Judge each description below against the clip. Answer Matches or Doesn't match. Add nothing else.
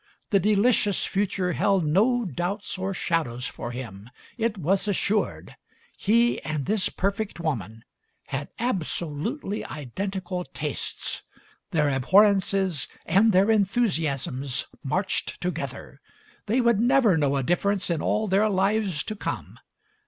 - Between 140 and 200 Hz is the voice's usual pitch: Matches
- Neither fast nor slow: Doesn't match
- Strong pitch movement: Matches